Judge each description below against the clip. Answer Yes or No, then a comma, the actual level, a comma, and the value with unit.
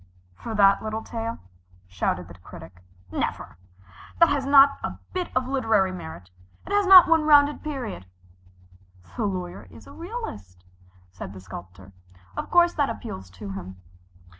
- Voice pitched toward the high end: Yes, high, 215 Hz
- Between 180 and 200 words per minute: No, average, 150 wpm